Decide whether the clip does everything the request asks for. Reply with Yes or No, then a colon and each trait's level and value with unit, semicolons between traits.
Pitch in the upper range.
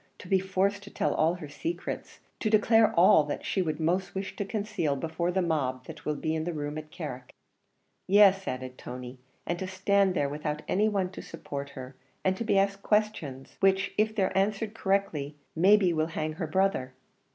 No: medium, 180 Hz